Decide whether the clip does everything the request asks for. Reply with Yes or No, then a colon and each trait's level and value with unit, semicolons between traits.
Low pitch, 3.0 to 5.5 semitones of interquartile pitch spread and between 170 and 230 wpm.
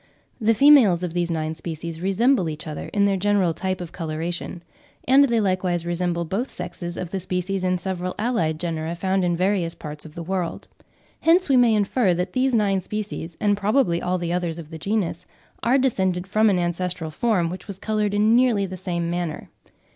No: medium, 185 Hz; average, 3.4 semitones; average, 195 wpm